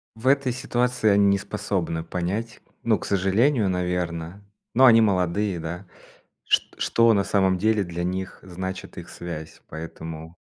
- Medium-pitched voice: No, very low, 95 Hz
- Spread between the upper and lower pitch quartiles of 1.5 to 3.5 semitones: No, average, 4.0 semitones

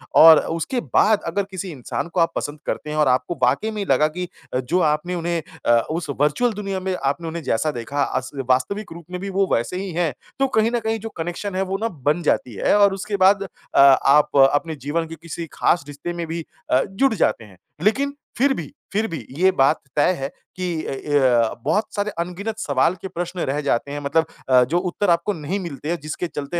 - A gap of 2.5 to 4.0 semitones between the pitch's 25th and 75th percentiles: No, average, 4.9 semitones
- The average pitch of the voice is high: No, medium, 170 Hz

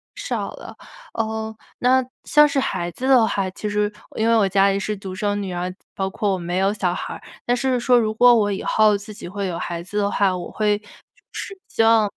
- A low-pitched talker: No, high, 205 Hz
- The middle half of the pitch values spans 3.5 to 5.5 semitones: No, narrow, 2.6 semitones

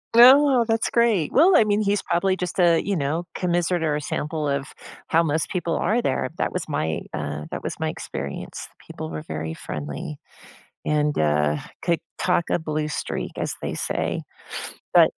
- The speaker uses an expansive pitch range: Yes, wide, 5.8 semitones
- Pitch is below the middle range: No, medium, 165 Hz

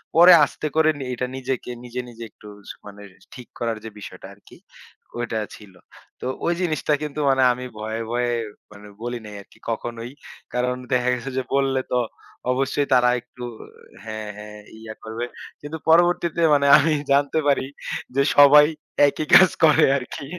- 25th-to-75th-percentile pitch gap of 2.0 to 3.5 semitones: No, average, 3.9 semitones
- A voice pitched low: Yes, low, 125 Hz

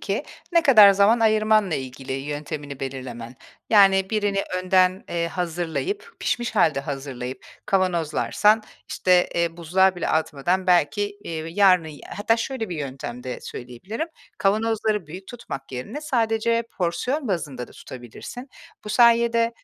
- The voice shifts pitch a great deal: Yes, wide, 6.7 semitones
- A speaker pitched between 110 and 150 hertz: No, medium, 185 Hz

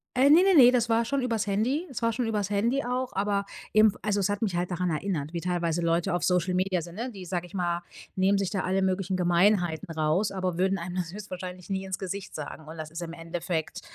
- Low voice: No, high, 190 Hz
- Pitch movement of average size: Yes, average, 3.4 semitones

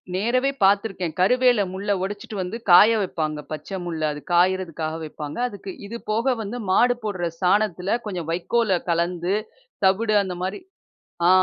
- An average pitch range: Yes, average, 3.6 semitones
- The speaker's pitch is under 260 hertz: Yes, high, 190 Hz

